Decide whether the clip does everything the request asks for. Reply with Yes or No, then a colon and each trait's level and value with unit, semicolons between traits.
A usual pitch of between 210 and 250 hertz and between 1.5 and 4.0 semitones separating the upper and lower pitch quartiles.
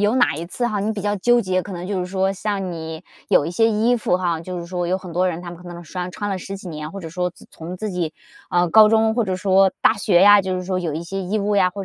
No: medium, 185 Hz; average, 2.7 semitones